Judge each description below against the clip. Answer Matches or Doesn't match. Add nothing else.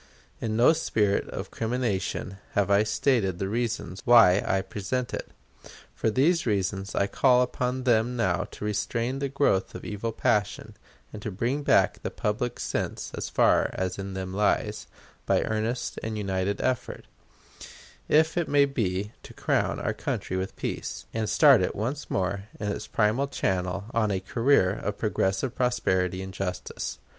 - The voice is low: Matches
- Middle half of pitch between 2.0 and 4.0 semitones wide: Doesn't match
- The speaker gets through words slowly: Doesn't match